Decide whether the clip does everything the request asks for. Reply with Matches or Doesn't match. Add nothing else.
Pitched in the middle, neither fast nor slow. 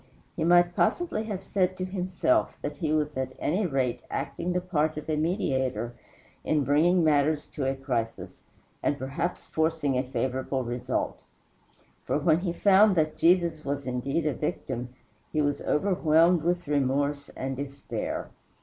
Matches